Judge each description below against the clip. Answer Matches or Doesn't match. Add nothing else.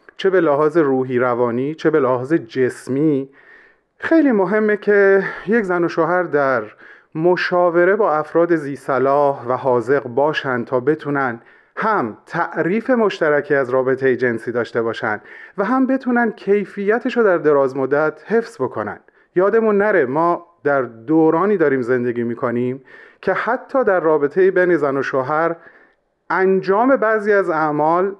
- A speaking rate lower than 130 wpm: Doesn't match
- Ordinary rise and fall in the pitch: Doesn't match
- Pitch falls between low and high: Matches